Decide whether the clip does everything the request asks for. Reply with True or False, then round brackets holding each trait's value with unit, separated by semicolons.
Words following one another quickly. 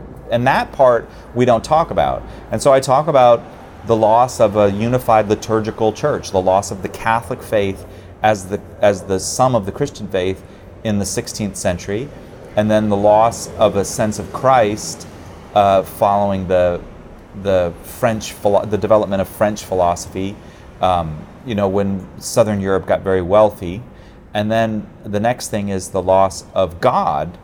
False (170 wpm)